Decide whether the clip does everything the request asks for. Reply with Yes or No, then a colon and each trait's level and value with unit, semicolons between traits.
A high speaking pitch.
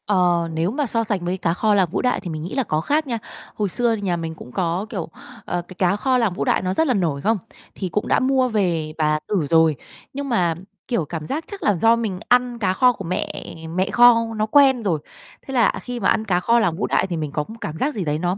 Yes: high, 195 Hz